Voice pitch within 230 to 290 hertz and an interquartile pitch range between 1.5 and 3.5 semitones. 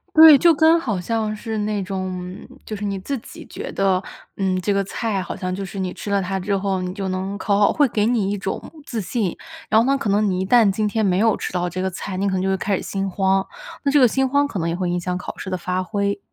No: high, 200 Hz; narrow, 2.6 semitones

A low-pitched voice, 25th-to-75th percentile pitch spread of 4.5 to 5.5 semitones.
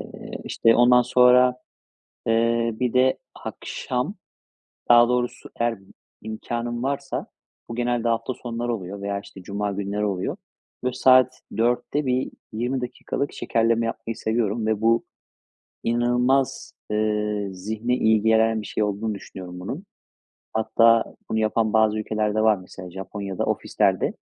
No: low, 115 Hz; narrow, 2.5 semitones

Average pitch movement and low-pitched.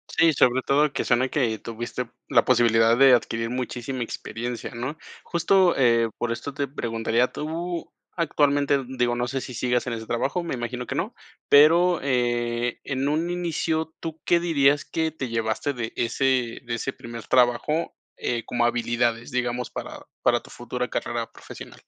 Yes: average, 3.7 semitones; low, 125 Hz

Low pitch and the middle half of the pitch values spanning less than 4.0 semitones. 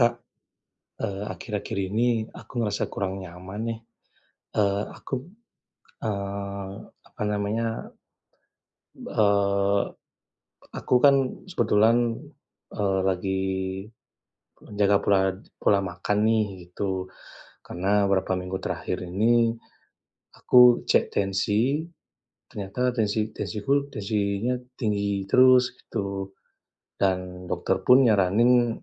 Yes: low, 105 Hz; average, 3.0 semitones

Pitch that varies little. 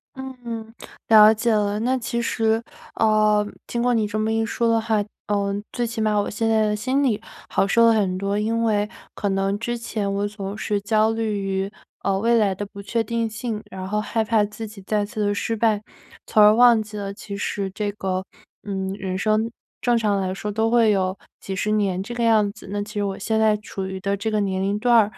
Yes: narrow, 2.0 semitones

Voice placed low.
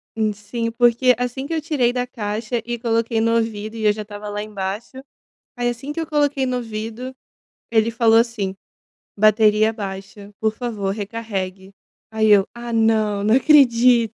No: high, 225 Hz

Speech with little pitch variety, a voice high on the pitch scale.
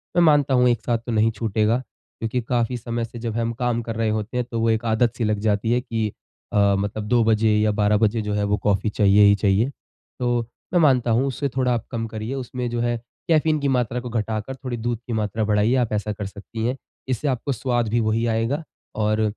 No: narrow, 2.3 semitones; low, 115 Hz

